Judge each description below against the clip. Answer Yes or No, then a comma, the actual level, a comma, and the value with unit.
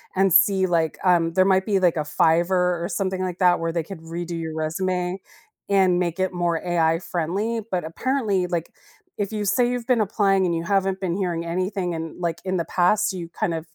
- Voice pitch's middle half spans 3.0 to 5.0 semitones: No, narrow, 2.5 semitones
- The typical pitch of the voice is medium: Yes, medium, 180 Hz